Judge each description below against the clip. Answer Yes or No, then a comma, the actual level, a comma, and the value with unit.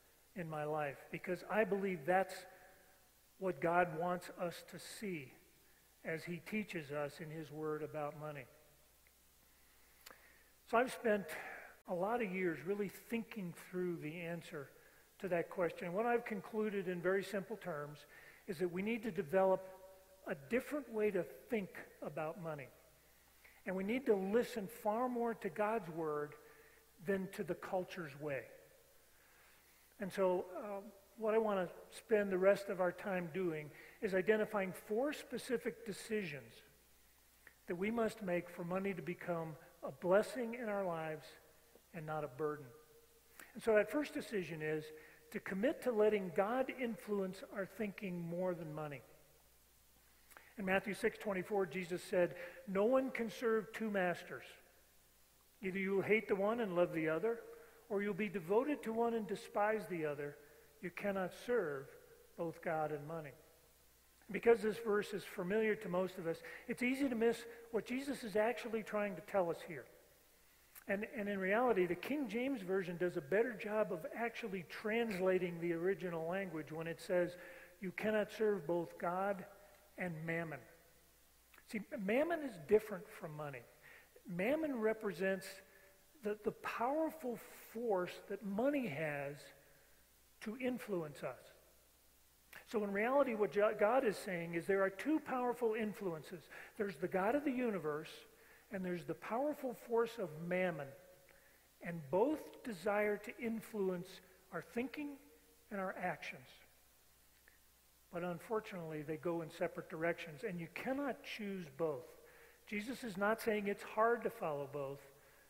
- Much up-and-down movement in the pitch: No, average, 4.6 semitones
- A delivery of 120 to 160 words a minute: Yes, average, 150 wpm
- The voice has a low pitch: No, high, 190 Hz